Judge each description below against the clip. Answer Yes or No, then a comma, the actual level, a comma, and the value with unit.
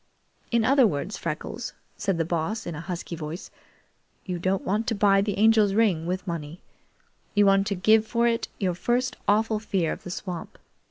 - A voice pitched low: No, high, 195 Hz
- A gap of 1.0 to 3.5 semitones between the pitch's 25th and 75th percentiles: No, average, 4.1 semitones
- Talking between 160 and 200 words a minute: Yes, average, 185 wpm